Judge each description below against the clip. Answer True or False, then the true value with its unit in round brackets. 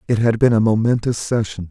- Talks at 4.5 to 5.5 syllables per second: False (5.8 syllables/s)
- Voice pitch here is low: True (110 Hz)